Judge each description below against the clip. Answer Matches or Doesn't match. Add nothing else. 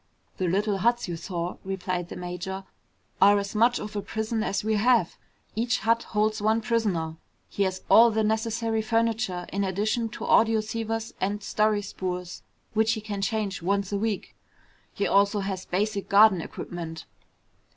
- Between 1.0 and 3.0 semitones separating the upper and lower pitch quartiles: Matches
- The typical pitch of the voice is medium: Doesn't match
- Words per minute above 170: Doesn't match